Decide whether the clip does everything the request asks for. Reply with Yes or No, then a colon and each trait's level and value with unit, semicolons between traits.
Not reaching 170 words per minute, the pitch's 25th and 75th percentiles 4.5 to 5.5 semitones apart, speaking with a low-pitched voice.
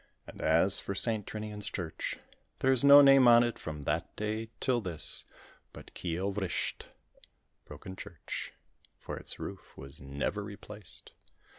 Yes: average, 145 wpm; average, 5.2 semitones; low, 105 Hz